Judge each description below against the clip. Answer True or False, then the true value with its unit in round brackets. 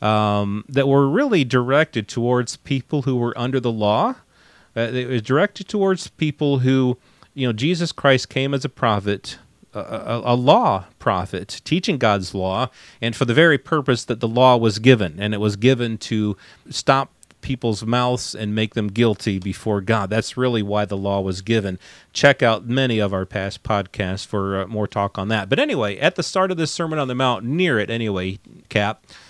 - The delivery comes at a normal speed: True (190 wpm)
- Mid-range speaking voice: False (120 Hz)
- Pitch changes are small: False (4.3 semitones)